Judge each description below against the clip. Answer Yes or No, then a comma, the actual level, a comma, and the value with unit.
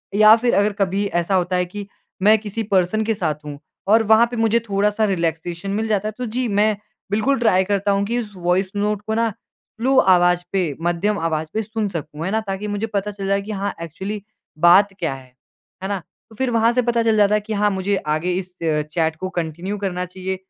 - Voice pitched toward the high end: Yes, high, 200 Hz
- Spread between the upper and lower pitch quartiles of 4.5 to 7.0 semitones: No, average, 3.2 semitones